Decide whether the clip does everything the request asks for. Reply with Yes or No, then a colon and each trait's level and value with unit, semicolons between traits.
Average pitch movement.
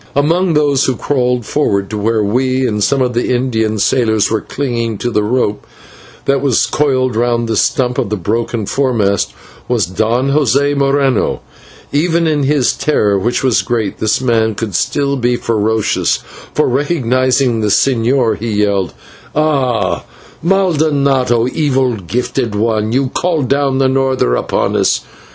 Yes: average, 3.9 semitones